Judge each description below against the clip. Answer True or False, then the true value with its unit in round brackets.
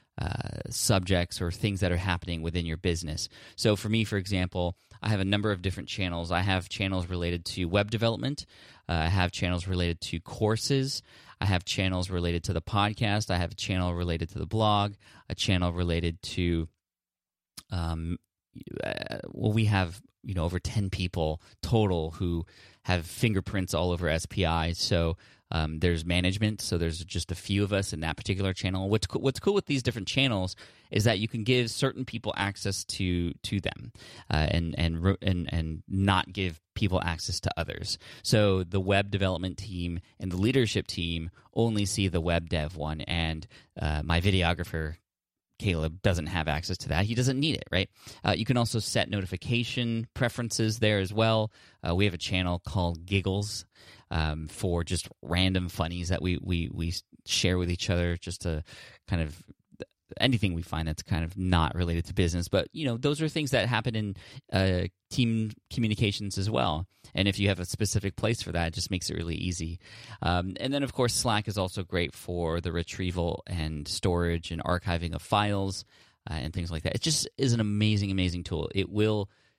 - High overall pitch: False (95 Hz)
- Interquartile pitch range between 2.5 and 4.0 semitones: True (3.7 semitones)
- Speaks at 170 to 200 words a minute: True (195 wpm)